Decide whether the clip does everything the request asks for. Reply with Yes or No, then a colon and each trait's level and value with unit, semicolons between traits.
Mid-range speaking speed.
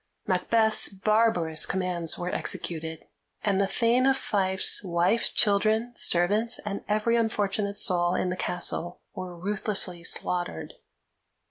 No: slow, 120 wpm